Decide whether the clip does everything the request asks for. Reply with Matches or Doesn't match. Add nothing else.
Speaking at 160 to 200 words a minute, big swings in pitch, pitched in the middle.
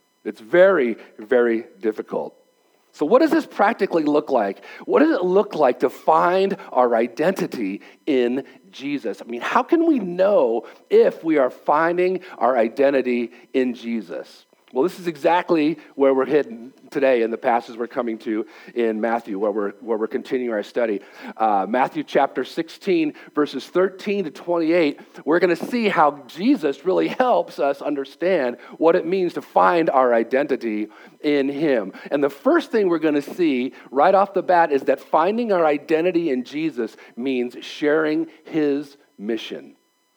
Matches